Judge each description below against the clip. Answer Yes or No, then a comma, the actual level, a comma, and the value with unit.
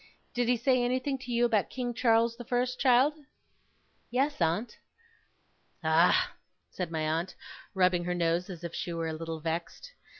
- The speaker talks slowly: No, average, 165 wpm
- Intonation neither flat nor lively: No, wide, 6.7 semitones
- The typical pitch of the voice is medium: No, high, 225 Hz